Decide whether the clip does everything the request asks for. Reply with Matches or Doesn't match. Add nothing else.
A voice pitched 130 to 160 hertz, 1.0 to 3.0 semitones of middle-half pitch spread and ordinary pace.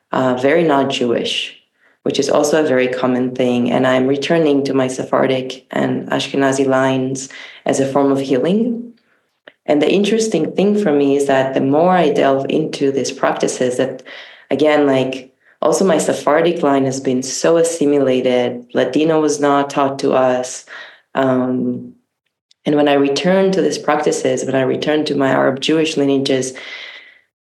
Matches